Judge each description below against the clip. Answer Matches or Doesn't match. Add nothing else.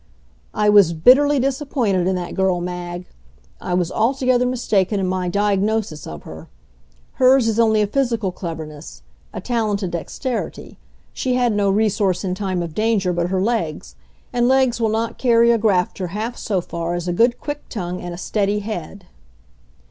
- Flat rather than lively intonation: Doesn't match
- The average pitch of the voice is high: Matches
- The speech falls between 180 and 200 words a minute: Doesn't match